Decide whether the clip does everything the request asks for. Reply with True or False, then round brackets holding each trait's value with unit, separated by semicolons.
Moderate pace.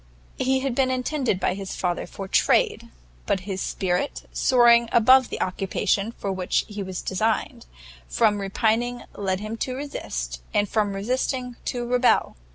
True (155 wpm)